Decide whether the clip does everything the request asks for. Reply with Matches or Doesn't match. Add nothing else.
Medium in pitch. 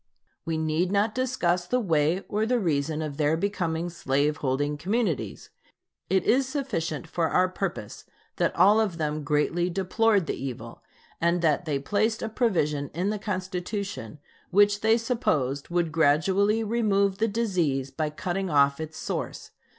Matches